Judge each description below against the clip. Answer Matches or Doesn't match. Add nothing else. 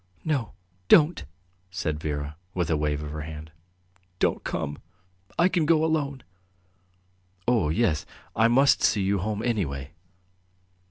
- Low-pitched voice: Matches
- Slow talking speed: Matches